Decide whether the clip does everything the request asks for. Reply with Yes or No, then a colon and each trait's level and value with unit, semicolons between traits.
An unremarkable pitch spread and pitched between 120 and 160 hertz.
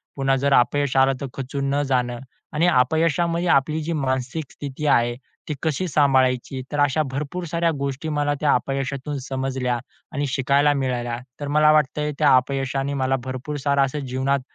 No: narrow, 2.2 semitones; medium, 140 Hz